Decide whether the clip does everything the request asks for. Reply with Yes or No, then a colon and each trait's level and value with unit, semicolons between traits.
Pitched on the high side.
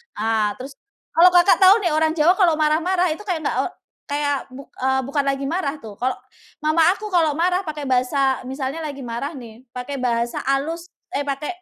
Yes: very high, 285 Hz